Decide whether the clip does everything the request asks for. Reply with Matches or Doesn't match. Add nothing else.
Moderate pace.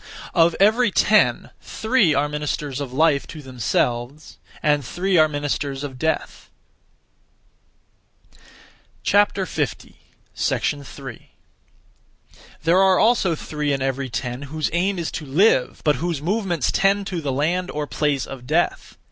Doesn't match